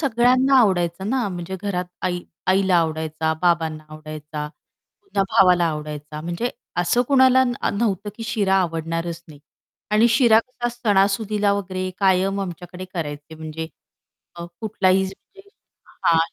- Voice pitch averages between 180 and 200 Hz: Yes, medium, 185 Hz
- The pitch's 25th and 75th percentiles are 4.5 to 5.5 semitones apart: Yes, average, 5.0 semitones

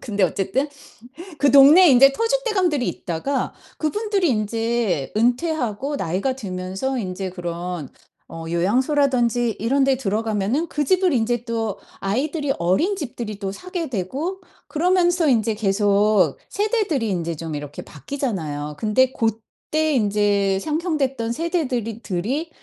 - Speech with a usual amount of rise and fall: No, wide, 7.1 semitones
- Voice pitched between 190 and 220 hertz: No, high, 235 Hz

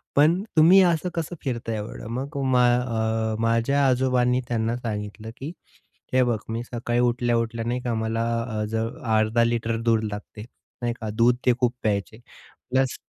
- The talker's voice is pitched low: Yes, low, 120 Hz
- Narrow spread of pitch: Yes, narrow, 2.1 semitones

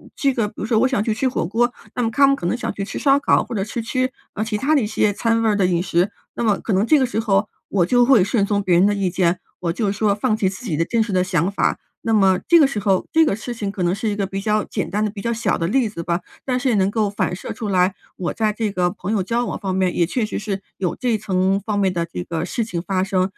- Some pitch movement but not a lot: Yes, average, 3.5 semitones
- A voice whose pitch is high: Yes, high, 205 Hz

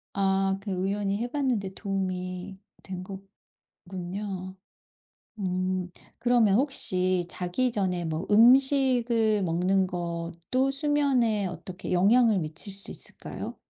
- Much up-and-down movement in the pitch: No, average, 4.1 semitones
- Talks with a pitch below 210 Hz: Yes, high, 195 Hz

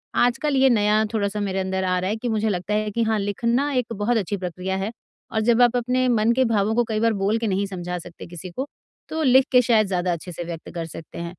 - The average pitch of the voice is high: Yes, high, 215 Hz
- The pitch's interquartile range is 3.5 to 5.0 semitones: Yes, average, 4.0 semitones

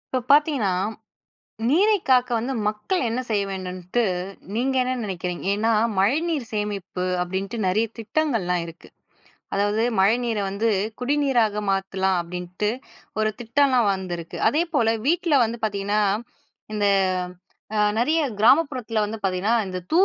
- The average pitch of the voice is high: Yes, high, 220 Hz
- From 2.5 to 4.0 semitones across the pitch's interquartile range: No, average, 4.9 semitones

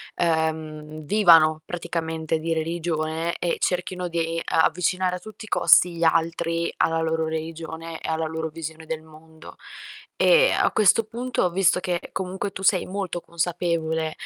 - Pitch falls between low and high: Yes, medium, 165 Hz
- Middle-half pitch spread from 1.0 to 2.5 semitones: Yes, narrow, 1.9 semitones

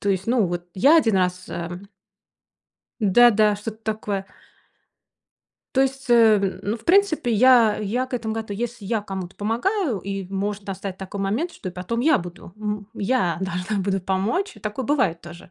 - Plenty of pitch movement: No, average, 3.8 semitones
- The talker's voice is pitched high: Yes, high, 210 Hz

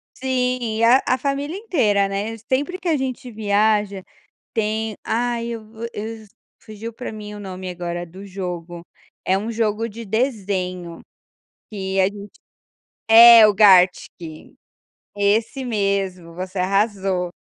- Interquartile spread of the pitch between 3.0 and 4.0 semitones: Yes, average, 3.4 semitones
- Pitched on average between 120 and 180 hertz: No, high, 210 Hz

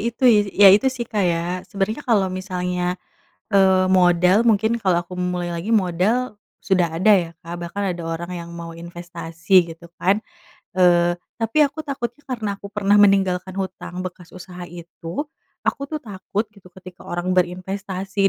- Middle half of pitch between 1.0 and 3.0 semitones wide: Yes, narrow, 2.5 semitones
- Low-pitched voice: No, medium, 185 Hz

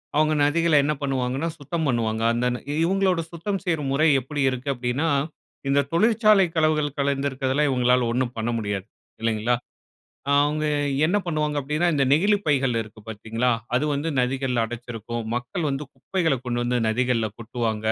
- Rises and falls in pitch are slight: No, average, 4.2 semitones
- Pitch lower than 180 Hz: Yes, low, 135 Hz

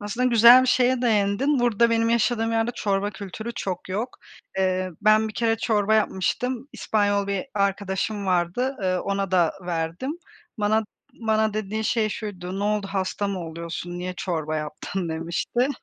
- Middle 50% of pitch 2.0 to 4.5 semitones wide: Yes, average, 3.4 semitones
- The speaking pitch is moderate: No, high, 205 Hz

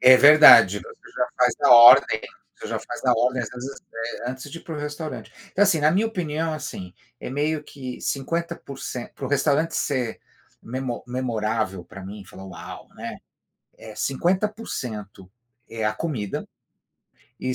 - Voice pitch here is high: No, low, 130 Hz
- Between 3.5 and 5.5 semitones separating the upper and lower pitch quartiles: Yes, average, 5.1 semitones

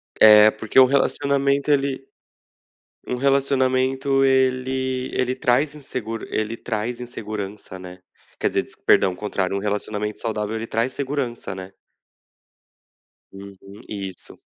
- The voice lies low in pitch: Yes, low, 120 Hz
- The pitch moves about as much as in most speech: Yes, average, 4.0 semitones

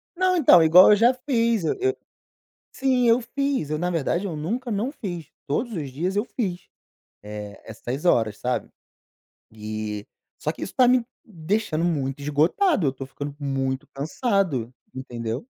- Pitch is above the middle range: No, medium, 170 Hz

